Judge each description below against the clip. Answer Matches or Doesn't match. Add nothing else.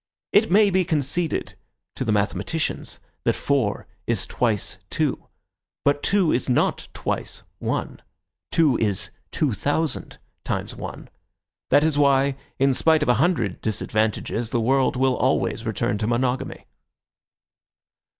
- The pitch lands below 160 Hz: Matches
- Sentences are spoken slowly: Matches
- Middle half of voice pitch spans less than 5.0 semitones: Doesn't match